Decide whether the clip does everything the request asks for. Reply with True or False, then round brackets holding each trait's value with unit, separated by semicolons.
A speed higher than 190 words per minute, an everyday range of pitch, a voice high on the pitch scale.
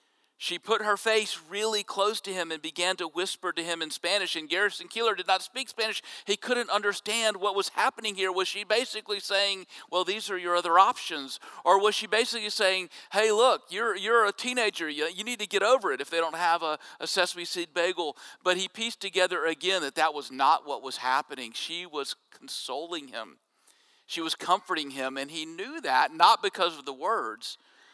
True (205 wpm; 3.9 semitones; 195 Hz)